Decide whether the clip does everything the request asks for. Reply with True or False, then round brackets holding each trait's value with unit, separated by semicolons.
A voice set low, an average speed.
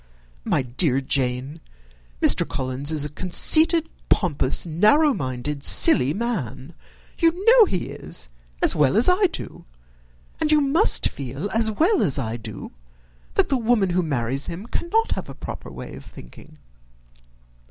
False (170 Hz; 150 wpm)